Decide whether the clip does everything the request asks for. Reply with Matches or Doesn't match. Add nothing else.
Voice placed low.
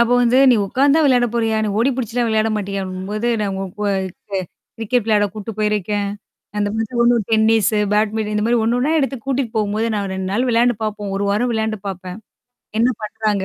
Doesn't match